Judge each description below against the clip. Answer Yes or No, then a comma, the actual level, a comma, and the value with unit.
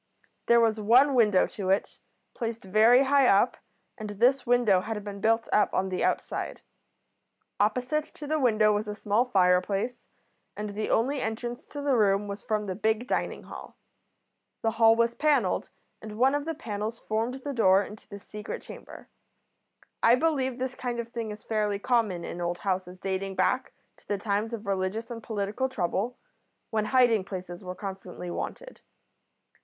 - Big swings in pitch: No, average, 3.6 semitones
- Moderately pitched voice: No, high, 220 Hz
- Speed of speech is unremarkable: Yes, average, 170 wpm